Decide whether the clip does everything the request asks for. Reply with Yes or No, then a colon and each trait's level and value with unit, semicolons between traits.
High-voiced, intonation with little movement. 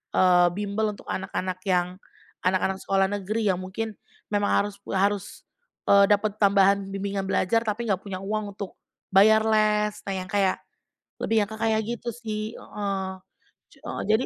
Yes: high, 200 Hz; narrow, 1.9 semitones